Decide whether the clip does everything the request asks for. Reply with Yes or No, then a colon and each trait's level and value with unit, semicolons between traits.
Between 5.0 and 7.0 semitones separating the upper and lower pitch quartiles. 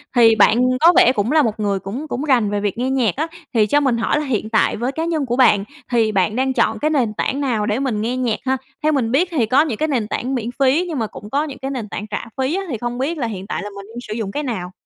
No: average, 4.3 semitones